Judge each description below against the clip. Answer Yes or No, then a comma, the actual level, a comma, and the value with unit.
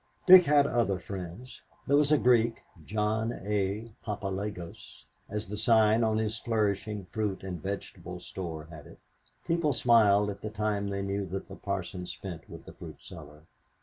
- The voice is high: No, low, 105 Hz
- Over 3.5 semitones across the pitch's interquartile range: No, average, 2.7 semitones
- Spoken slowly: No, average, 165 wpm